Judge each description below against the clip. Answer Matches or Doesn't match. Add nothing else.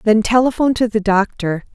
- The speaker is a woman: Matches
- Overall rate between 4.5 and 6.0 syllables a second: Matches